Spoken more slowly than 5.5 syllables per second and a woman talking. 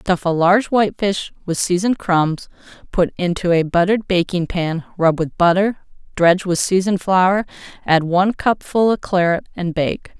Yes: 5.0 syllables/s; female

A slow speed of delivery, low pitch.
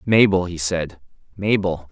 Yes: slow, 125 wpm; very low, 90 Hz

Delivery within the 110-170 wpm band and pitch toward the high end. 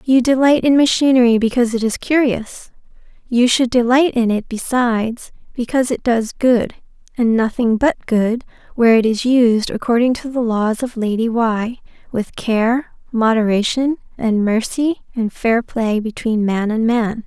Yes: average, 155 wpm; high, 235 Hz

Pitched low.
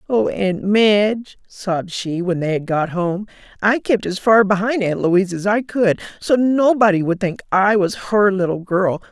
No: high, 200 Hz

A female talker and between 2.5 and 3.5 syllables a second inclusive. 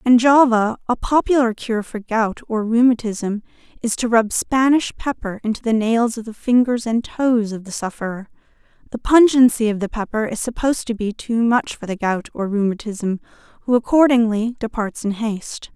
No: female; 5.0 syllables/s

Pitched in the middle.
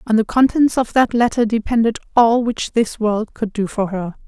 No: high, 225 Hz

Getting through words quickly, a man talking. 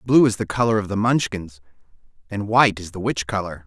Yes: fast, 215 wpm; male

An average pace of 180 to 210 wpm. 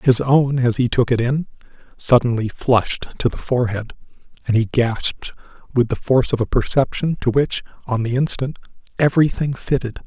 No: average, 165 wpm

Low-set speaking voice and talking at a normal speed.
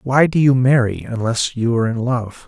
Yes: low, 125 Hz; average, 170 wpm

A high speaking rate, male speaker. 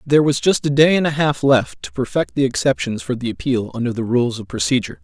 Yes: fast, 250 wpm; male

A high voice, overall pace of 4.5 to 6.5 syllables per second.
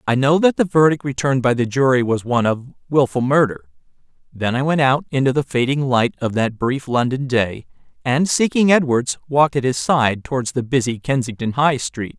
No: low, 130 Hz; 5.3 syllables/s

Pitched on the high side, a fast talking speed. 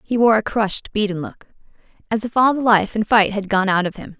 Yes: high, 210 Hz; fast, 255 wpm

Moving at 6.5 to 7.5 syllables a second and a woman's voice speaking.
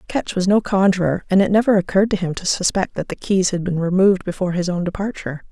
Yes: 6.6 syllables/s; female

